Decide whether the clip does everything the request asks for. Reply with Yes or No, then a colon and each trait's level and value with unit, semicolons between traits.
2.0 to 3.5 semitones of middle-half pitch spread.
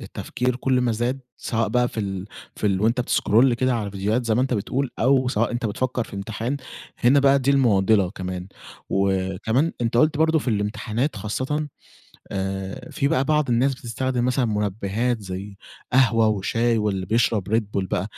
No: average, 4.1 semitones